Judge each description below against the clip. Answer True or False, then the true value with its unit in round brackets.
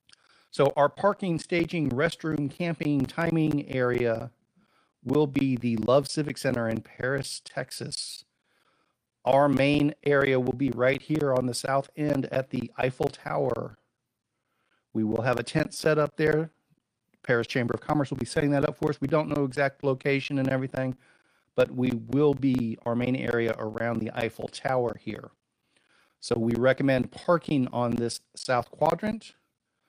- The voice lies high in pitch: False (135 Hz)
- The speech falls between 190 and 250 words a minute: False (155 wpm)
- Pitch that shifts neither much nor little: True (3.6 semitones)